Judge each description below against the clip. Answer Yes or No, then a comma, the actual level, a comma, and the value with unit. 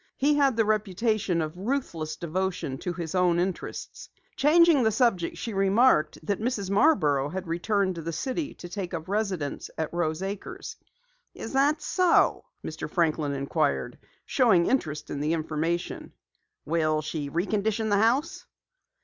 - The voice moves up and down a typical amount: No, wide, 5.7 semitones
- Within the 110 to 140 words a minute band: No, average, 150 wpm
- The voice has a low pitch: No, high, 190 Hz